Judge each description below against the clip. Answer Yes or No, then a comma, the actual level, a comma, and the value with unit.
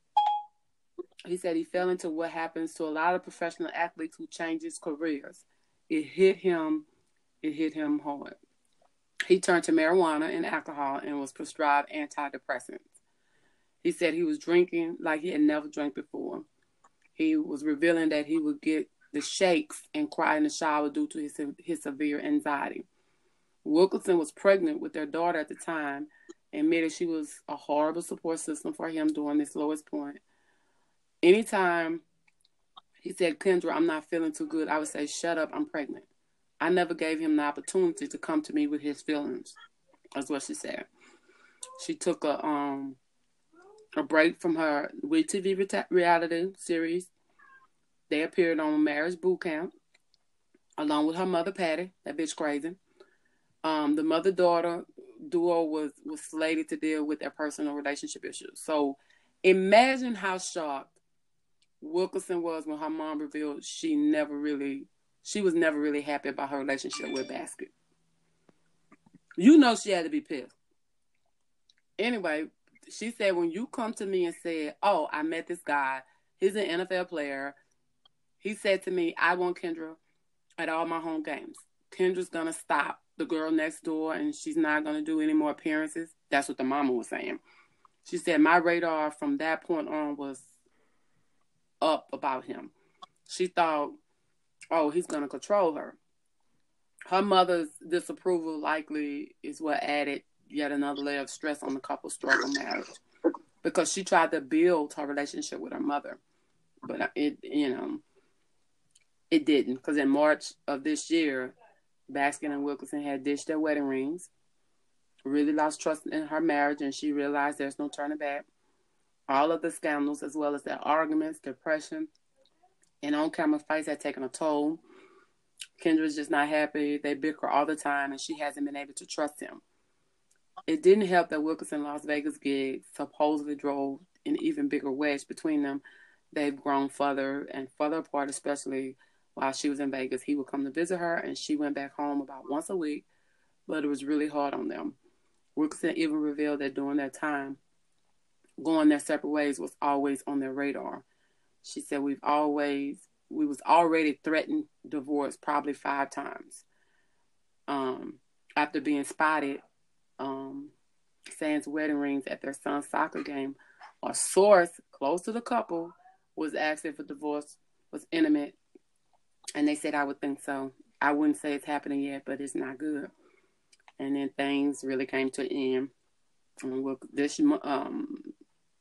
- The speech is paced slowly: No, average, 165 wpm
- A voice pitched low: No, medium, 160 Hz